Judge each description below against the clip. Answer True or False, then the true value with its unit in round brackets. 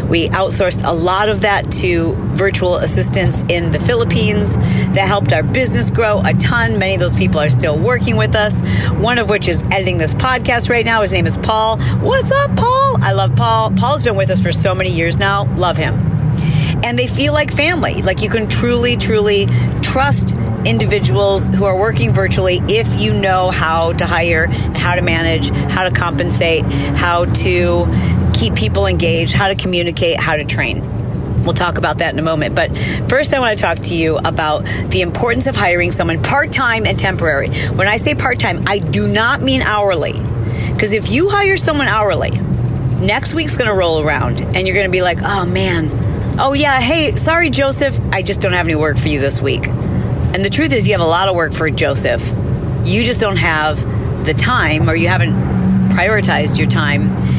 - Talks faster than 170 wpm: True (200 wpm)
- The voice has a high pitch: False (115 Hz)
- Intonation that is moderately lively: False (7.7 semitones)